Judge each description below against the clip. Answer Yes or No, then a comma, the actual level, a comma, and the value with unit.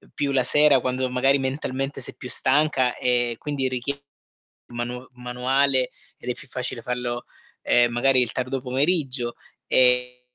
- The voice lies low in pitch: Yes, low, 130 Hz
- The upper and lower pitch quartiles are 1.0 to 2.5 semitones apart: Yes, narrow, 1.6 semitones